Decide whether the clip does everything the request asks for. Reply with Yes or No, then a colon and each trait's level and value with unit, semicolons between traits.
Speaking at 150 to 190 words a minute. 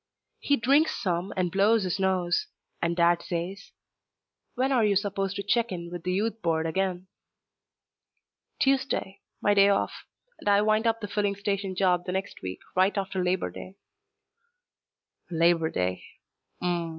Yes: average, 160 wpm